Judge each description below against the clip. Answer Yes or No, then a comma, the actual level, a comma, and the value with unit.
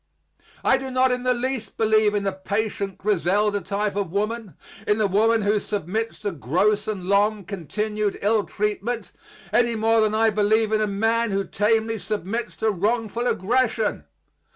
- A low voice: No, high, 215 Hz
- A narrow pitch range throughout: Yes, narrow, 2.0 semitones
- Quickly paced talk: No, average, 165 wpm